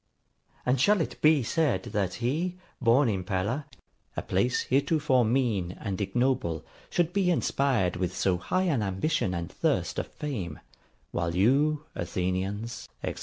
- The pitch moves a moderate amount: No, wide, 7.8 semitones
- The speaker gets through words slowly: No, average, 145 wpm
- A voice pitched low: Yes, low, 120 Hz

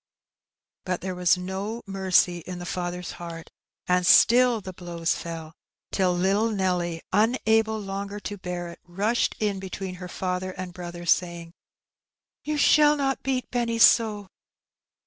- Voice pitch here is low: No, medium, 185 Hz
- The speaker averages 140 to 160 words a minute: Yes, average, 145 wpm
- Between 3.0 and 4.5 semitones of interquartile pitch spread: Yes, average, 3.5 semitones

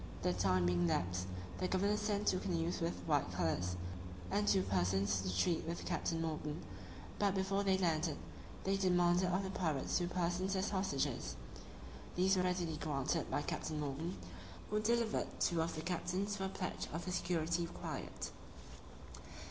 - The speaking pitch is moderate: Yes, medium, 170 Hz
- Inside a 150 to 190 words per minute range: Yes, average, 165 wpm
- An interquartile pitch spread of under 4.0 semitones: No, average, 5.3 semitones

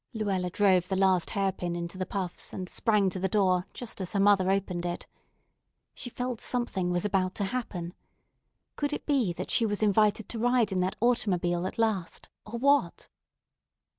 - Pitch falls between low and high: No, high, 195 Hz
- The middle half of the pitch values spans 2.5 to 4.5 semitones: Yes, average, 3.4 semitones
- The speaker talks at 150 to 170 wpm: No, average, 190 wpm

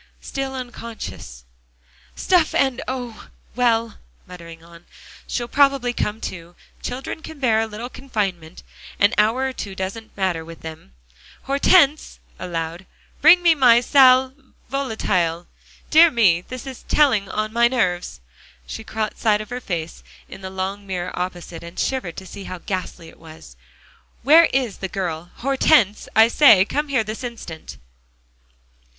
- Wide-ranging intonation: Yes, wide, 6.4 semitones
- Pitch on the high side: Yes, high, 220 Hz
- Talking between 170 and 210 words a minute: No, average, 145 wpm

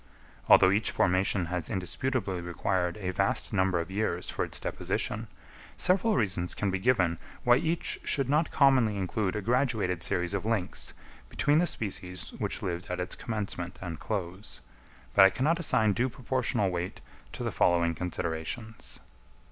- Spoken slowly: No, average, 155 wpm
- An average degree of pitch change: Yes, average, 4.9 semitones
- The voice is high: No, very low, 95 Hz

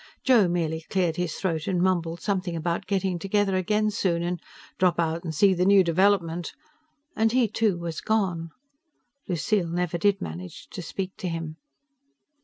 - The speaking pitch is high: No, medium, 180 Hz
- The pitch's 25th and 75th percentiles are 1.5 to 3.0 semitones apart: Yes, average, 2.7 semitones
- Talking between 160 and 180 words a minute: Yes, average, 165 wpm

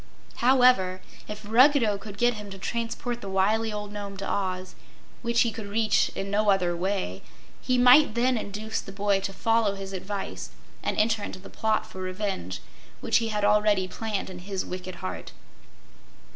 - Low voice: No, high, 205 Hz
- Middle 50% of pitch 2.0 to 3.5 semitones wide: Yes, average, 2.7 semitones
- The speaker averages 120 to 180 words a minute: Yes, average, 175 wpm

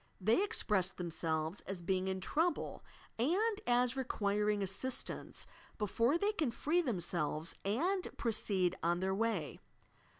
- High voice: Yes, high, 210 Hz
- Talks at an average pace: No, slow, 125 wpm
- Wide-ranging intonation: Yes, wide, 6.2 semitones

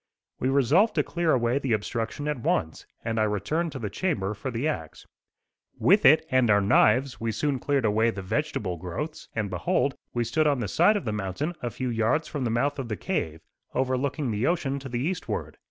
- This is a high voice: No, low, 125 Hz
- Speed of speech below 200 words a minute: No, fast, 205 wpm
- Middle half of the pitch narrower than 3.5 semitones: No, wide, 5.4 semitones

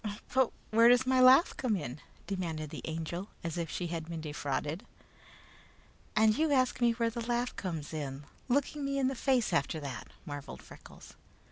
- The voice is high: Yes, high, 200 Hz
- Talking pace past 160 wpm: Yes, average, 175 wpm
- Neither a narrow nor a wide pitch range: No, wide, 8.1 semitones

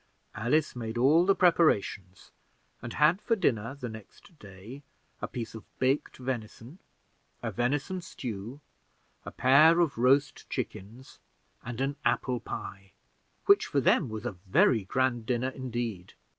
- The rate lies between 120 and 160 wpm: Yes, average, 140 wpm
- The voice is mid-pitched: No, low, 125 Hz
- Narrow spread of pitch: No, average, 4.3 semitones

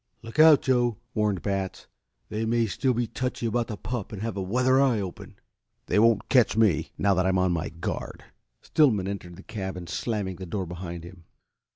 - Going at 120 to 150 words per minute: No, average, 195 wpm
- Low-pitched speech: Yes, low, 105 Hz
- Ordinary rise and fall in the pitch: Yes, average, 4.0 semitones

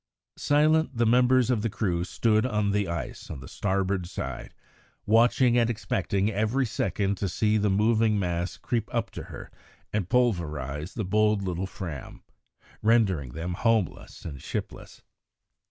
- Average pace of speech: Yes, average, 150 wpm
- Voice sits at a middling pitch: No, low, 105 Hz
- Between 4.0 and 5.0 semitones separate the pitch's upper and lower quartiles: Yes, average, 4.3 semitones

